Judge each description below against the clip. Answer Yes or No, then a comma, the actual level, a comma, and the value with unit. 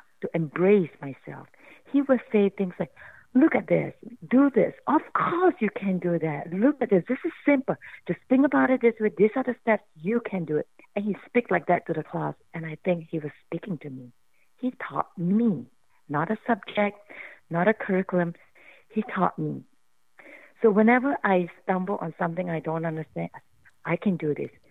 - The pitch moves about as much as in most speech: No, wide, 5.9 semitones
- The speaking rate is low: No, average, 195 wpm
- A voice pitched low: No, high, 190 Hz